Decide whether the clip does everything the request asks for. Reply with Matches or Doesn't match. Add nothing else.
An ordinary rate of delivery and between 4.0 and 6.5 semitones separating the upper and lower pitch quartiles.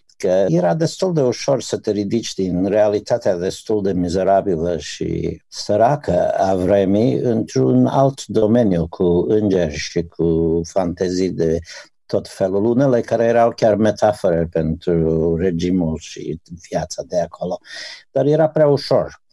Matches